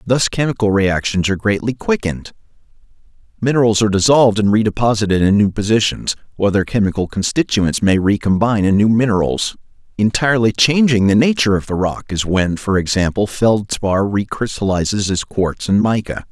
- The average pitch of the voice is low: Yes, low, 105 Hz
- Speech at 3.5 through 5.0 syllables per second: No, 5.6 syllables/s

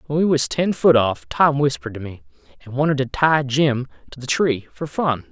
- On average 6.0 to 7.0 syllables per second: No, 5.2 syllables/s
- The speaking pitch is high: No, low, 135 Hz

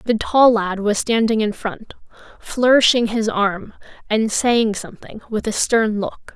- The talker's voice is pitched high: Yes, high, 220 Hz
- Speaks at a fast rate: No, average, 160 wpm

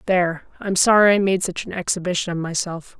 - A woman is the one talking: Yes, female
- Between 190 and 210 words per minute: Yes, average, 200 wpm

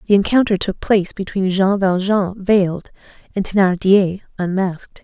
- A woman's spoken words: Yes, female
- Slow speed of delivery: Yes, slow, 130 wpm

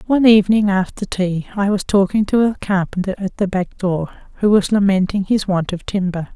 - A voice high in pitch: Yes, high, 195 Hz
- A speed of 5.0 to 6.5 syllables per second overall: Yes, 5.4 syllables/s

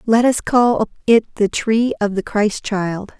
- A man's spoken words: No, female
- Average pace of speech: Yes, average, 190 wpm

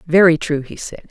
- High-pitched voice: No, medium, 165 Hz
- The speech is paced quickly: Yes, fast, 215 wpm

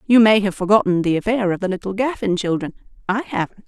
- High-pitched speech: Yes, high, 200 Hz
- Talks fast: Yes, fast, 210 wpm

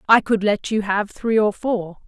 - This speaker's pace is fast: Yes, fast, 230 wpm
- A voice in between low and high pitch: No, high, 210 Hz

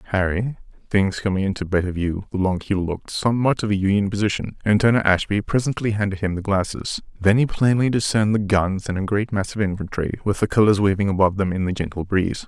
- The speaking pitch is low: Yes, low, 100 Hz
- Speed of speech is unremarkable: No, fast, 220 wpm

